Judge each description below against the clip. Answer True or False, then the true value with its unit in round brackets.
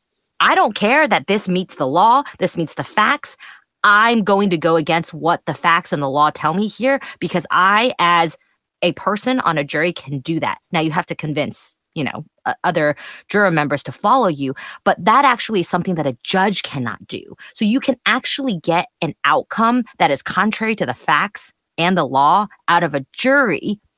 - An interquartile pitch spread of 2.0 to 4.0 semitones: False (4.8 semitones)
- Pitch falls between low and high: True (180 Hz)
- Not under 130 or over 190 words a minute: False (200 wpm)